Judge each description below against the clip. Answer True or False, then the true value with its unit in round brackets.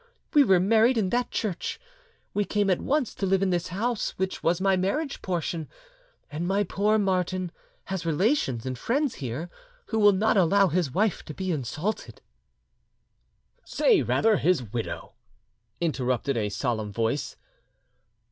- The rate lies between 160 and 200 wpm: False (150 wpm)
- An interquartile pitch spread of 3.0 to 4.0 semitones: False (5.3 semitones)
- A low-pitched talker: False (185 Hz)